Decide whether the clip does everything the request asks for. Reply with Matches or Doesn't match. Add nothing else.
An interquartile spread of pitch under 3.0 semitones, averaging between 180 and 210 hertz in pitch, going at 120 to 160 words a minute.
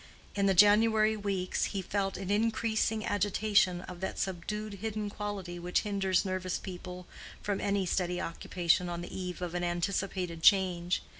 Matches